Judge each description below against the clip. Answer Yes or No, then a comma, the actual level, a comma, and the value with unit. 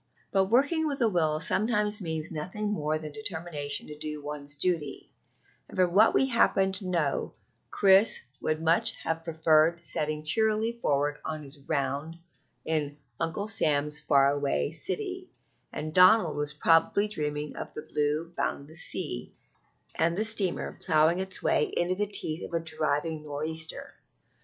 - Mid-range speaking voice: Yes, medium, 160 Hz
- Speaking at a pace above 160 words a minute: No, average, 150 wpm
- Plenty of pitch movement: No, average, 4.3 semitones